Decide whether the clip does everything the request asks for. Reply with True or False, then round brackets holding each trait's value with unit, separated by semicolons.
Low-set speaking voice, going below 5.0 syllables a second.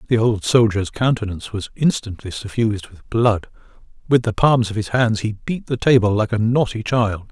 False (110 Hz; 5.1 syllables/s)